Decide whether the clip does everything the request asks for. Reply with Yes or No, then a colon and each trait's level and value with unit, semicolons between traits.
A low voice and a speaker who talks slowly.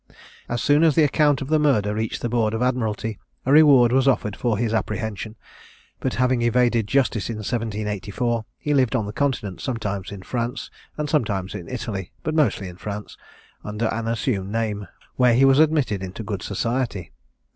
No: low, 115 Hz; average, 180 wpm